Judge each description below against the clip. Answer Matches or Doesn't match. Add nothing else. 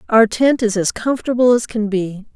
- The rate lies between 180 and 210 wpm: Matches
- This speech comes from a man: Doesn't match